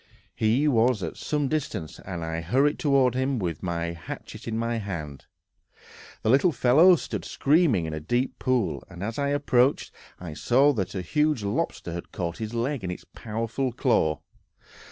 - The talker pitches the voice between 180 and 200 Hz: No, low, 115 Hz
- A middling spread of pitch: No, wide, 7.6 semitones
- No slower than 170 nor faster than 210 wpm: Yes, average, 175 wpm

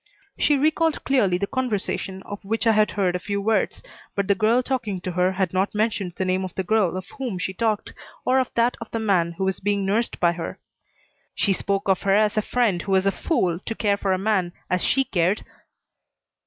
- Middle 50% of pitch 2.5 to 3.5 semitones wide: Yes, average, 3.1 semitones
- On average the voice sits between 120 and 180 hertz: No, high, 200 Hz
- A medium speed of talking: No, fast, 225 wpm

